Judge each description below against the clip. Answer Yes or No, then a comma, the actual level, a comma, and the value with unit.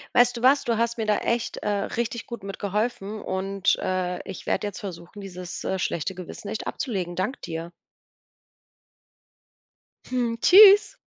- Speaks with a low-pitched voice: No, high, 205 Hz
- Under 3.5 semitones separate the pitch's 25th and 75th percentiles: No, average, 4.1 semitones